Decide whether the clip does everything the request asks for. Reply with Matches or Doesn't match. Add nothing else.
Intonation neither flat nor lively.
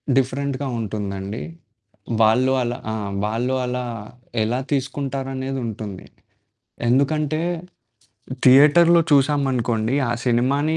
Matches